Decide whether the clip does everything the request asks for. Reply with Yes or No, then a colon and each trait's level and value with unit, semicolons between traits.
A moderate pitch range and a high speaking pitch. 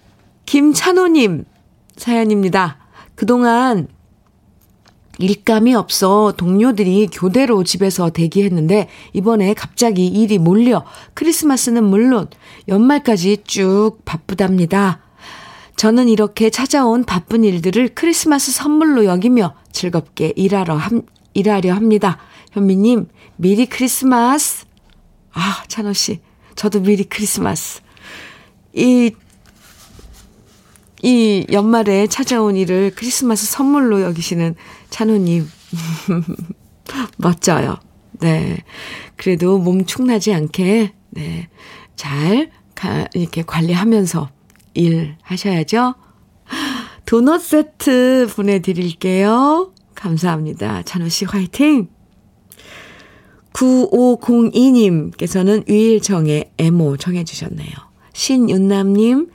Yes: average, 4.6 semitones; high, 205 Hz